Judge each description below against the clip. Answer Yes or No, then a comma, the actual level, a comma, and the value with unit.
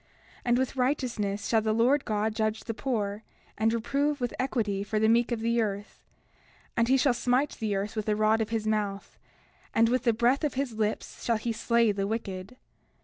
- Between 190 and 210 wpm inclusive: Yes, fast, 205 wpm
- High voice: Yes, high, 225 Hz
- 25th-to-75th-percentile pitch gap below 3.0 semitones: Yes, narrow, 2.5 semitones